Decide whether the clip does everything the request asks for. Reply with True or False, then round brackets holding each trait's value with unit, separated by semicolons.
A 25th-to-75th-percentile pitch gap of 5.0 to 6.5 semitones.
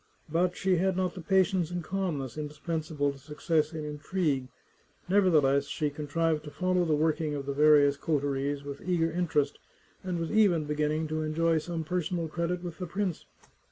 False (3.2 semitones)